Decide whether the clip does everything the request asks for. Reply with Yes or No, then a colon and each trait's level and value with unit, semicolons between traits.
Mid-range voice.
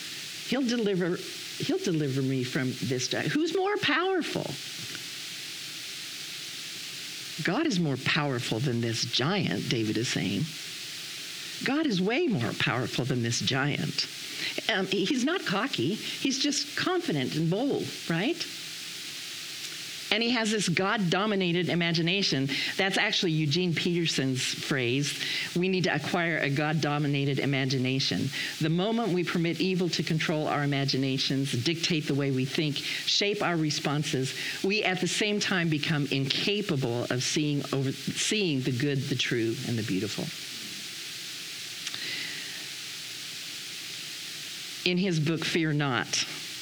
Yes: medium, 160 Hz